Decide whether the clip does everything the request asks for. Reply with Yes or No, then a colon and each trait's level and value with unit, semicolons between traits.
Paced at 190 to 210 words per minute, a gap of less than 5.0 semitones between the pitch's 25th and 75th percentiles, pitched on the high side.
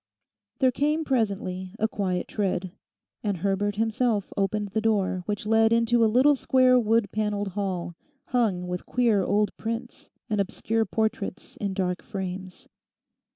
No: average, 145 wpm; average, 2.9 semitones; high, 210 Hz